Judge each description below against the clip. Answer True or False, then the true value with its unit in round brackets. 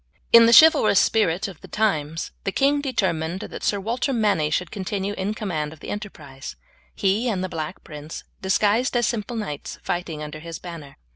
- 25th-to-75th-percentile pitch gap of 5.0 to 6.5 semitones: True (5.3 semitones)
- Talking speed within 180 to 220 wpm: True (185 wpm)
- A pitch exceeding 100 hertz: True (190 Hz)